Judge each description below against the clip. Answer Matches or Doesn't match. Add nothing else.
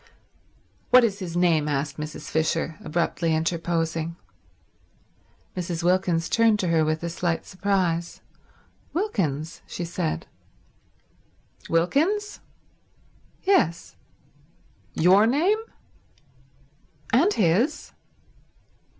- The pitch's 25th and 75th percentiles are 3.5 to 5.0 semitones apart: Matches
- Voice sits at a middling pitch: Matches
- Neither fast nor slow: Doesn't match